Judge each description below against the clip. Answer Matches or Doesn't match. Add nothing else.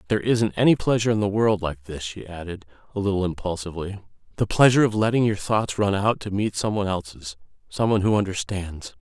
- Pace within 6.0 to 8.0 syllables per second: Matches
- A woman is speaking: Doesn't match